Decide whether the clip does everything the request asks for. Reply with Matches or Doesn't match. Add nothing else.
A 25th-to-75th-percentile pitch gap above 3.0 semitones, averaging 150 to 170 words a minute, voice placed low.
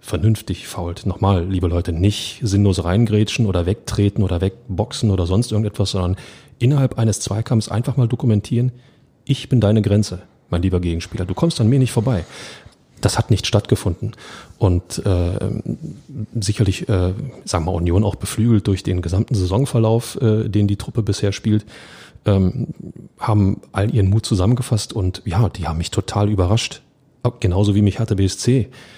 Matches